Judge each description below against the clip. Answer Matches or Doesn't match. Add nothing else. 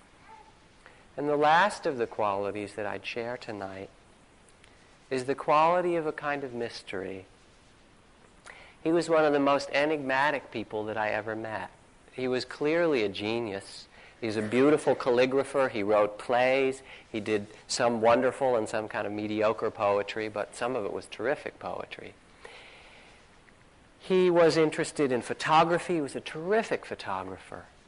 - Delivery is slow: Doesn't match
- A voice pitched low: Matches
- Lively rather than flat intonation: Matches